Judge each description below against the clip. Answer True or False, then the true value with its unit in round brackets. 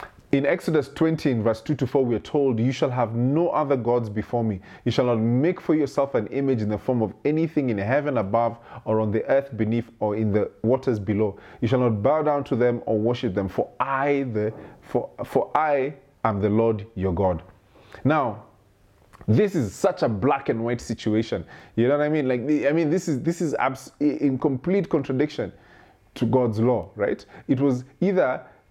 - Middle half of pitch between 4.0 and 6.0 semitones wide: True (4.6 semitones)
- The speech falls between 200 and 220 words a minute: True (205 wpm)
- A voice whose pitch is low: True (125 Hz)